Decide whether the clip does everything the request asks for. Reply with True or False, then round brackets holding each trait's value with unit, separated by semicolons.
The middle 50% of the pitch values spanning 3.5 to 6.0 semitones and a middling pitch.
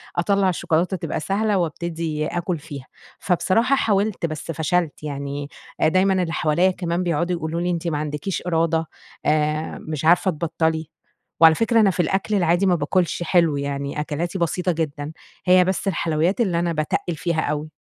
False (2.8 semitones; 170 Hz)